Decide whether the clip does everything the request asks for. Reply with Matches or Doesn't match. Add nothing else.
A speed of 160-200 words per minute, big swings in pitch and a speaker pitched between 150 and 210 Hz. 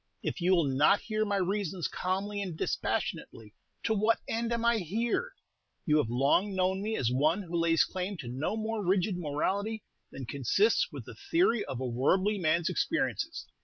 Matches